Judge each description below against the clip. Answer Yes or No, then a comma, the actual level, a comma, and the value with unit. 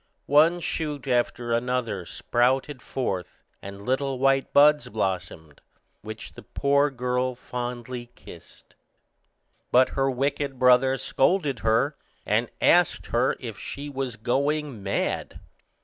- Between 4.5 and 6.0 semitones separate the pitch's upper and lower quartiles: No, average, 2.7 semitones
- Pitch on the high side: No, low, 130 Hz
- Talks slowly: Yes, slow, 115 wpm